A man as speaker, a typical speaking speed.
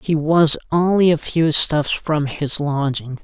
Yes: male; average, 165 wpm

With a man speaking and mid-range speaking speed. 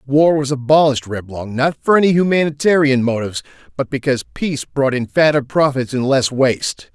Yes: male; average, 165 wpm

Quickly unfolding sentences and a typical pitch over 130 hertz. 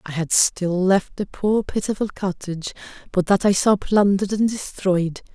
No: average, 170 wpm; high, 190 Hz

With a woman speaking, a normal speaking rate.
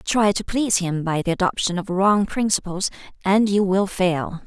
Yes: female; average, 190 wpm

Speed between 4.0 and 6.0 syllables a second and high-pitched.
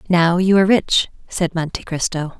No: 5.0 syllables/s; medium, 175 Hz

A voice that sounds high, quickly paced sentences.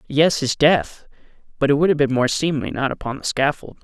No: medium, 140 Hz; fast, 220 wpm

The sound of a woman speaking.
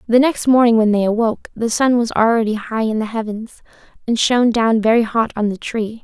Yes: female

